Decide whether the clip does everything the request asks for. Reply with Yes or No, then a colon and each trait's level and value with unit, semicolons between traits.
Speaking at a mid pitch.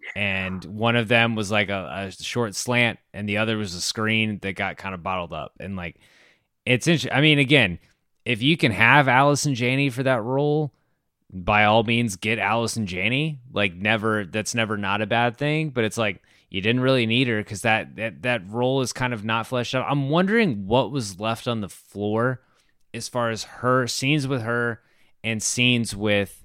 No: low, 115 Hz